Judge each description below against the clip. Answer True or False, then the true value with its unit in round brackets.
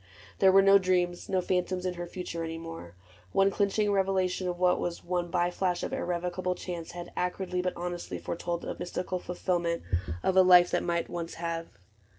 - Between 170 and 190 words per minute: True (185 wpm)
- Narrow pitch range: True (1.1 semitones)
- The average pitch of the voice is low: False (180 Hz)